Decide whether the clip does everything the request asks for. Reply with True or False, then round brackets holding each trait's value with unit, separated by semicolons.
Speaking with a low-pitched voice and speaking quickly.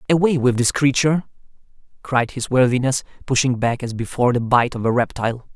False (125 Hz; 175 wpm)